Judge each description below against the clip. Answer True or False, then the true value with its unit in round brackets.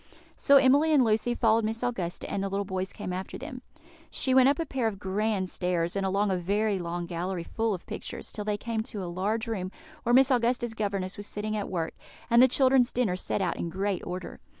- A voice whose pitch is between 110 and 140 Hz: False (210 Hz)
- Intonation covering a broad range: False (4.1 semitones)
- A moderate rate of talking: False (225 wpm)